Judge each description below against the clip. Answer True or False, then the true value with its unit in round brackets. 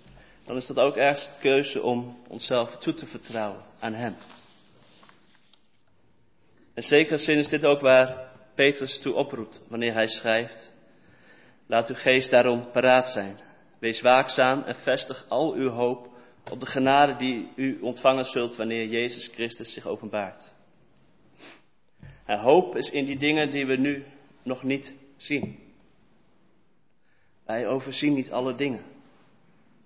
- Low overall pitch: True (130 Hz)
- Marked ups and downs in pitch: False (2.7 semitones)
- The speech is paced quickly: False (140 wpm)